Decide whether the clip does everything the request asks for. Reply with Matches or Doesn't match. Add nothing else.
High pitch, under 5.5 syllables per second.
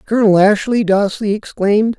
Matches